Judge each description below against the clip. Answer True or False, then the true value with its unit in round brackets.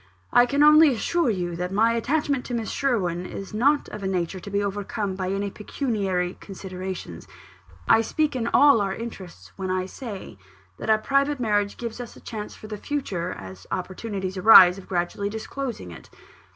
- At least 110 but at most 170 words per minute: False (180 wpm)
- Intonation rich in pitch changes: False (4.4 semitones)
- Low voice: False (205 Hz)